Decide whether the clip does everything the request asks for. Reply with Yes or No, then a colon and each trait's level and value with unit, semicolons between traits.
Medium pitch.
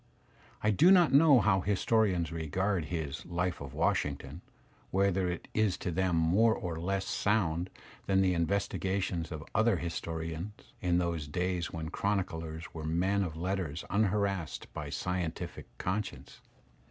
No: very low, 90 Hz